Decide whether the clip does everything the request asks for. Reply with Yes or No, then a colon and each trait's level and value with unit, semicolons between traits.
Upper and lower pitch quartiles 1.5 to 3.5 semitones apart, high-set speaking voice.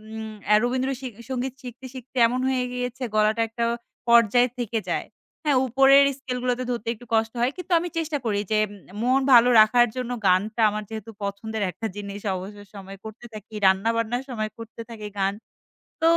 Yes: average, 2.8 semitones; high, 230 Hz